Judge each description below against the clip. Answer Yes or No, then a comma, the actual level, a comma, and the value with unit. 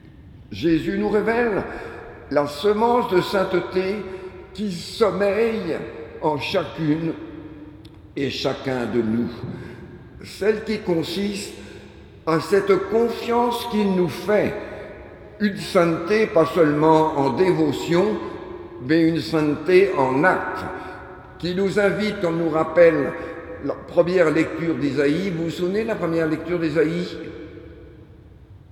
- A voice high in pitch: No, medium, 170 Hz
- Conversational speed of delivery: No, slow, 110 wpm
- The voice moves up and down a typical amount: Yes, average, 4.0 semitones